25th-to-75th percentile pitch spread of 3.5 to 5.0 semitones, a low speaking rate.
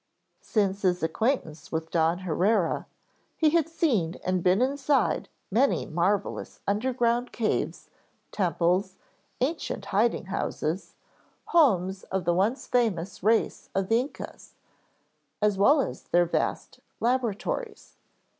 No: wide, 5.6 semitones; slow, 115 wpm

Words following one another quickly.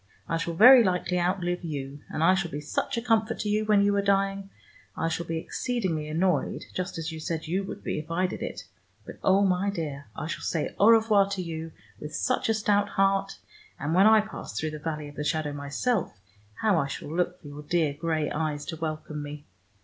Yes: fast, 225 wpm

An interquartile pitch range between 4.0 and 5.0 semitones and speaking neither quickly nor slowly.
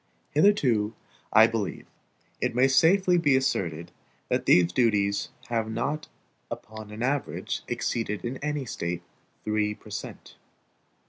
No: average, 4.7 semitones; slow, 125 wpm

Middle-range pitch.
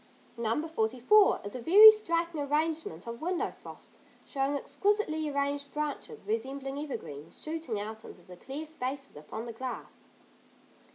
No: very high, 280 Hz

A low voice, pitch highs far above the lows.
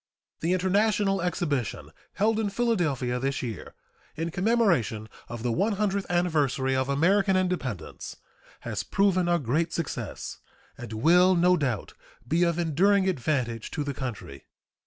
No: medium, 170 Hz; wide, 6.4 semitones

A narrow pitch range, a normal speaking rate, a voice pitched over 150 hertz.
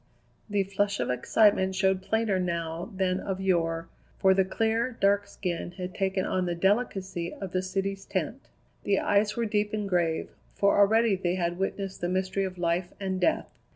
Yes: narrow, 1.9 semitones; average, 180 wpm; high, 190 Hz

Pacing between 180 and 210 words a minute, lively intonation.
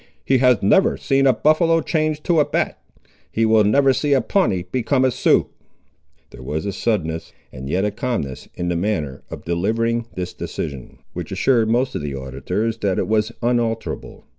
Yes: average, 185 wpm; wide, 6.7 semitones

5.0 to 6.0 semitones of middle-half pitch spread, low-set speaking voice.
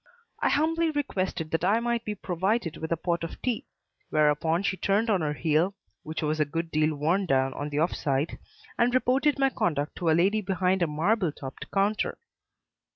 No: wide, 5.5 semitones; medium, 175 Hz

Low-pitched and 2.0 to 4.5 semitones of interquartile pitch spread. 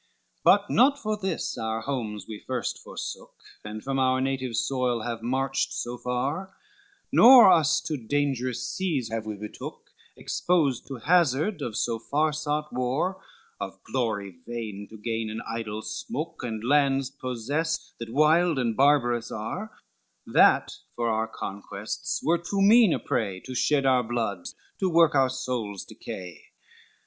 No: low, 130 Hz; average, 5.3 semitones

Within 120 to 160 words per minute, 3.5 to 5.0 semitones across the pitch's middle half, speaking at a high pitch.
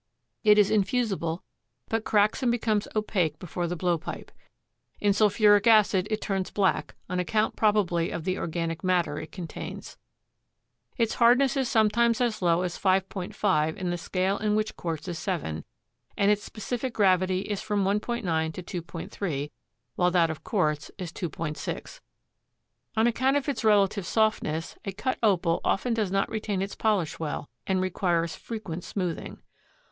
Yes: average, 155 wpm; average, 3.8 semitones; high, 195 Hz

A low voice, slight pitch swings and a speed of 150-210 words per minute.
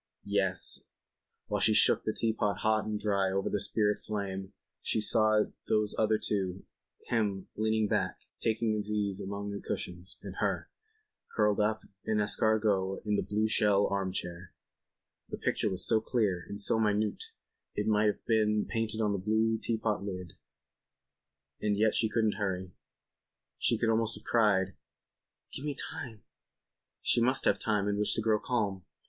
Yes: low, 105 Hz; narrow, 1.7 semitones; average, 165 wpm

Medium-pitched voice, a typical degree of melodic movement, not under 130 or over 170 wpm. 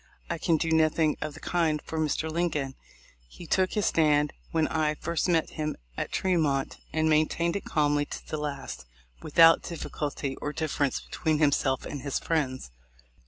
No: medium, 155 Hz; narrow, 2.0 semitones; average, 165 wpm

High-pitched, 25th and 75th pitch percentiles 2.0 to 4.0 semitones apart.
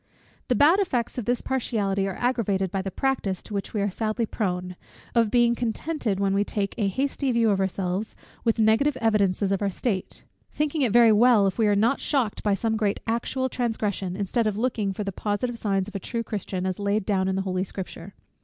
Yes: high, 210 Hz; average, 3.4 semitones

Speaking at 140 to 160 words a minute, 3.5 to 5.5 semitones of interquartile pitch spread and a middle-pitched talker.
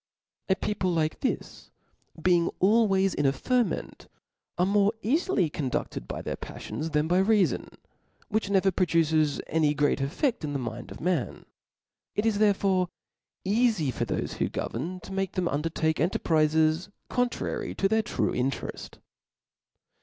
Yes: average, 150 wpm; average, 4.7 semitones; medium, 180 Hz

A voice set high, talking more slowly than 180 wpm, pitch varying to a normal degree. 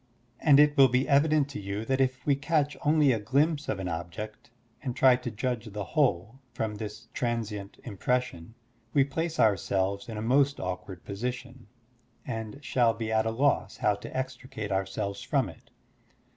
No: low, 120 Hz; average, 170 wpm; average, 4.6 semitones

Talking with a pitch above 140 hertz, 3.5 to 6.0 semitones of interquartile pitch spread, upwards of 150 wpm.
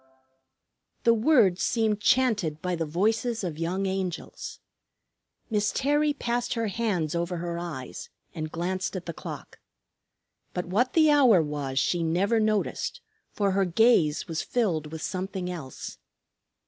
No: high, 190 Hz; average, 5.1 semitones; average, 140 wpm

